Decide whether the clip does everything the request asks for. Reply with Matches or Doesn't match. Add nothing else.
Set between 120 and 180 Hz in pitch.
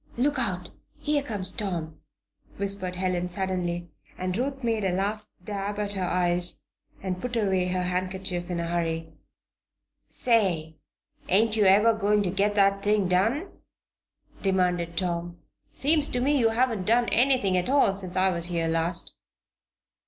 Doesn't match